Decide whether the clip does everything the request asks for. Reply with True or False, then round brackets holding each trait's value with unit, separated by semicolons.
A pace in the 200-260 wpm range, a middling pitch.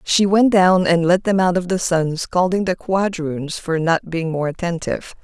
True (205 wpm; 175 Hz)